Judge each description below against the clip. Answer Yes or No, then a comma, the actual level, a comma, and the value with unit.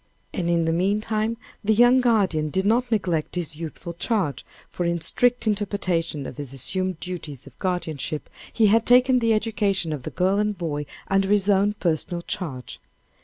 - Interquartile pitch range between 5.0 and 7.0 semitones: No, average, 4.4 semitones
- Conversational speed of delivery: Yes, average, 170 wpm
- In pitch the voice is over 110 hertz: Yes, medium, 185 Hz